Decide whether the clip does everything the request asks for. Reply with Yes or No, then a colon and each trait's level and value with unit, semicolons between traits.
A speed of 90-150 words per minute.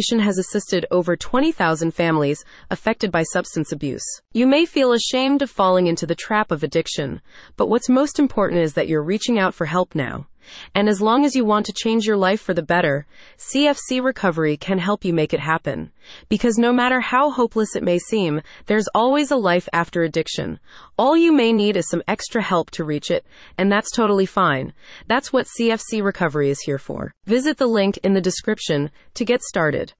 No: average, 195 wpm